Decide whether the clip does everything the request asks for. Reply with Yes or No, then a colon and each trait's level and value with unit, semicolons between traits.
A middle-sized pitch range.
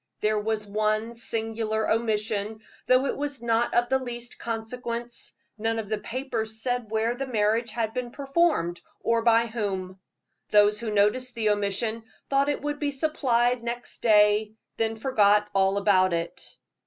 No: narrow, 2.3 semitones